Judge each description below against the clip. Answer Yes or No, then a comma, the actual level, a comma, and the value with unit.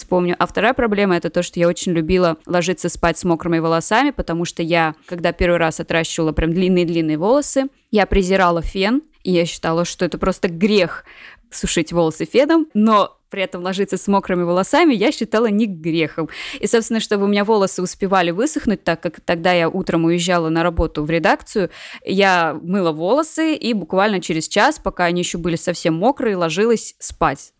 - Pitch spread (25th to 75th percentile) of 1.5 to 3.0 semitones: No, average, 3.6 semitones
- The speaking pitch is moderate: Yes, medium, 180 Hz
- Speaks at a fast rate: Yes, fast, 180 wpm